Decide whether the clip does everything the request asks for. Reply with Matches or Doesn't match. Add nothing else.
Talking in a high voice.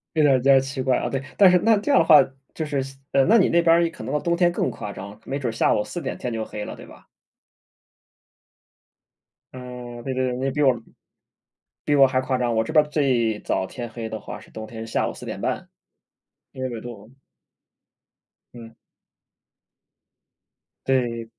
Doesn't match